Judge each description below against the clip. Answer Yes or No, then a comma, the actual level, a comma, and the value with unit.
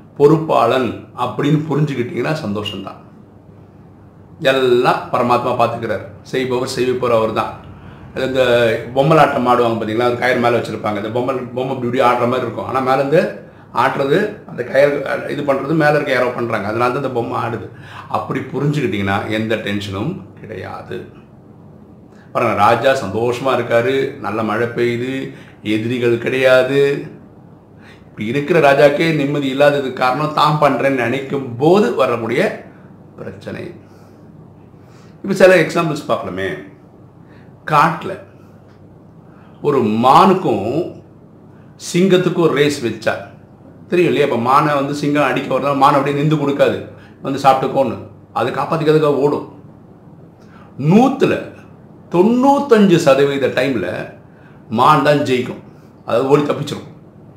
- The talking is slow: No, average, 100 wpm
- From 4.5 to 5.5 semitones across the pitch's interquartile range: No, average, 3.5 semitones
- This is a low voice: Yes, low, 130 Hz